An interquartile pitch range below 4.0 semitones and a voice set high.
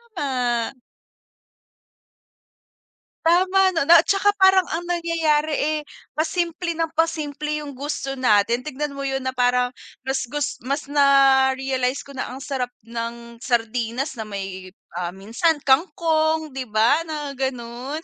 No: average, 4.3 semitones; very high, 275 Hz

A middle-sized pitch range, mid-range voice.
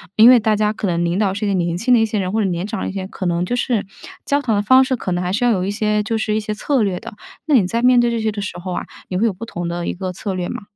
No: average, 3.7 semitones; high, 210 Hz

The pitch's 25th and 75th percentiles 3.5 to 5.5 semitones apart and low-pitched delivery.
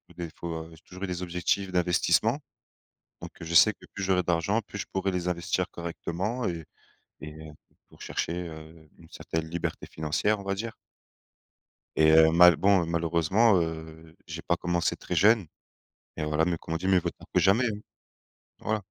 No: average, 2.9 semitones; very low, 85 Hz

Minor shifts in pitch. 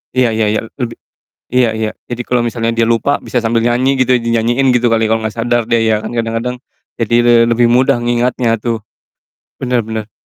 Yes: narrow, 1.3 semitones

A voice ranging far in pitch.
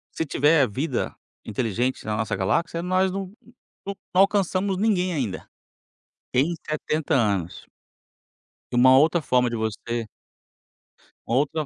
Yes: wide, 7.4 semitones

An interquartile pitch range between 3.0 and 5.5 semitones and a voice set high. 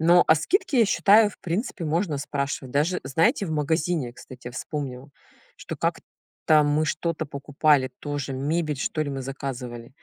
No: average, 3.5 semitones; medium, 150 Hz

